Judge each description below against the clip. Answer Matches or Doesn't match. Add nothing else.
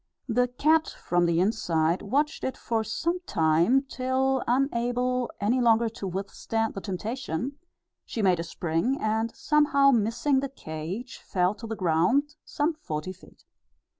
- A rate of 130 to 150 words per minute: Matches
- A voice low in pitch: Doesn't match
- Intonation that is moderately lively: Doesn't match